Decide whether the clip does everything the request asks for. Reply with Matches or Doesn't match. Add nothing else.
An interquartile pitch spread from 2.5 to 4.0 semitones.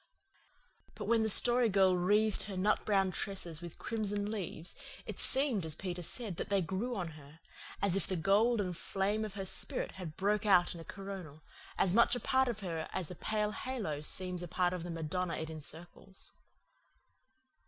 Matches